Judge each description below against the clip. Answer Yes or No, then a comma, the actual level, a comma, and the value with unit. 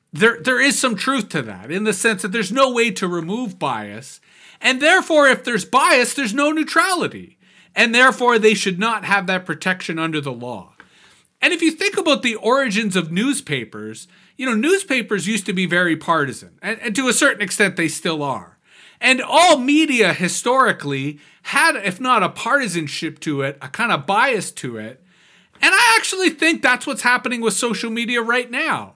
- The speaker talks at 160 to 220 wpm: Yes, average, 190 wpm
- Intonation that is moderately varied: No, wide, 6.8 semitones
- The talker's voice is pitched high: Yes, high, 220 Hz